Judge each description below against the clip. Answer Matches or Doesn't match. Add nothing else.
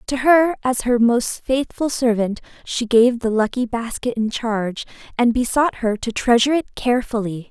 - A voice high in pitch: Matches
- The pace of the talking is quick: Doesn't match